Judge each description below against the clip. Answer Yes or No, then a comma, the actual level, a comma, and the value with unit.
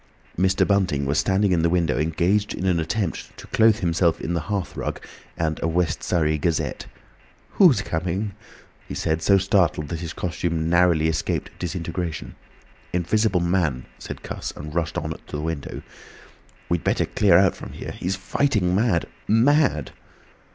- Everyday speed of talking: Yes, average, 160 wpm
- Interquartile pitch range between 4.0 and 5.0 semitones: No, average, 3.2 semitones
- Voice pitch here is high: No, very low, 85 Hz